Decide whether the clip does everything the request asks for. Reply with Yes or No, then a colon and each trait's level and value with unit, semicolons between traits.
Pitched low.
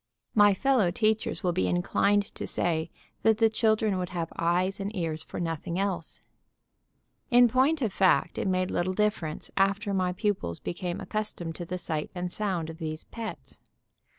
No: medium, 185 Hz